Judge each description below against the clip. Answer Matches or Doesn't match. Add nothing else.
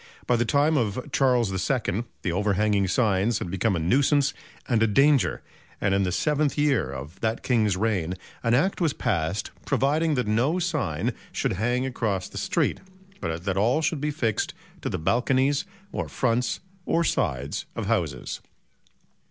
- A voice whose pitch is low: Matches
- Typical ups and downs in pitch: Doesn't match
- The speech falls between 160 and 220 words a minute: Matches